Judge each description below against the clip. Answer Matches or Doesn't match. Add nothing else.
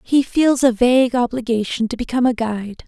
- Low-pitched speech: Doesn't match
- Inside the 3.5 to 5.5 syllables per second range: Doesn't match